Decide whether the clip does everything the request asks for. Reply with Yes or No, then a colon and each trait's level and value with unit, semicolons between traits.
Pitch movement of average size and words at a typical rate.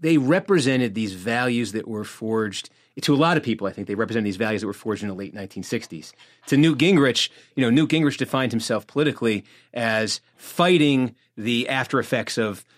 Yes: average, 4.3 semitones; average, 195 wpm